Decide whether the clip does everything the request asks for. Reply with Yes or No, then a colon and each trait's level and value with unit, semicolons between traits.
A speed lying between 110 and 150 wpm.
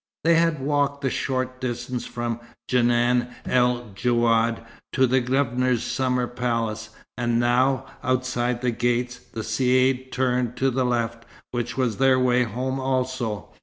Yes: average, 140 wpm